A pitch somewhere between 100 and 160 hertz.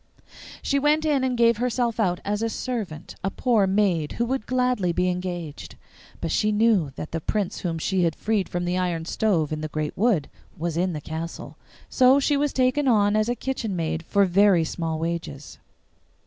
No: high, 195 Hz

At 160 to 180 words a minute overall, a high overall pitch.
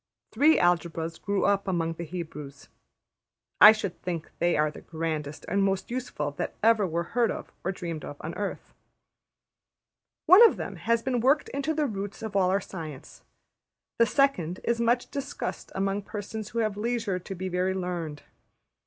Yes: average, 170 wpm; high, 195 Hz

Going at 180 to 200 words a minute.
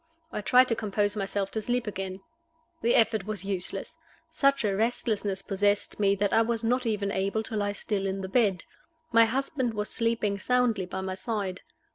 Yes: average, 185 wpm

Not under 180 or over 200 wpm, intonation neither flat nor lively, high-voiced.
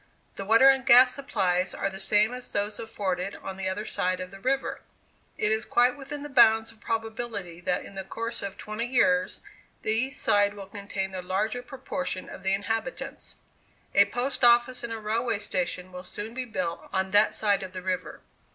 Yes: average, 195 wpm; average, 4.1 semitones; high, 215 Hz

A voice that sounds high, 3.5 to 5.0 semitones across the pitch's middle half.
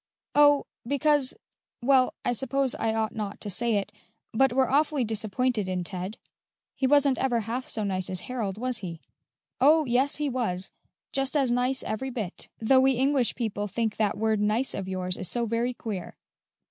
Yes: high, 235 Hz; average, 4.2 semitones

